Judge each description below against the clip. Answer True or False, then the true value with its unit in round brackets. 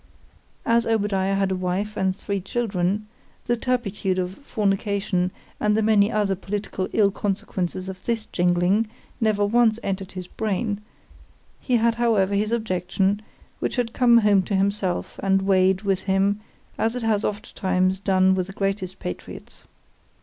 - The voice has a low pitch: False (200 Hz)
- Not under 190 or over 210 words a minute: False (145 wpm)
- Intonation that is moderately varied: False (2.3 semitones)